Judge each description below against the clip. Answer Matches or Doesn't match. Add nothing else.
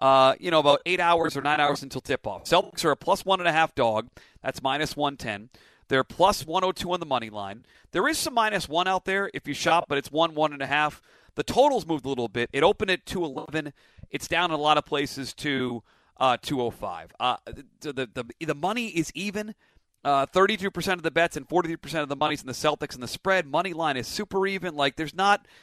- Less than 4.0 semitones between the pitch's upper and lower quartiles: Doesn't match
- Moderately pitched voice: Matches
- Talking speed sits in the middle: Doesn't match